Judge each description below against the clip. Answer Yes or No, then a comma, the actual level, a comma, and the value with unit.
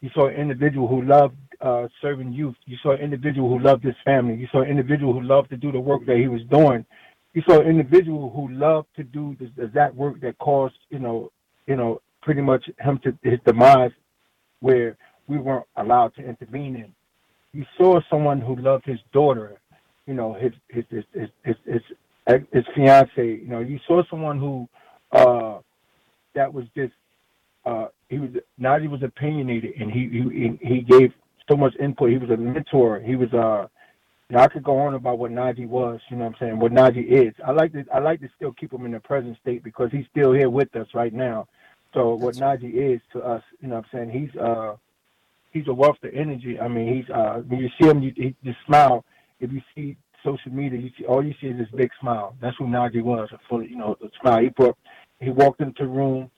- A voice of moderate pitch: No, low, 130 Hz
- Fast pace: Yes, fast, 220 wpm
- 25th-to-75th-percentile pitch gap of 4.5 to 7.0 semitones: No, average, 2.8 semitones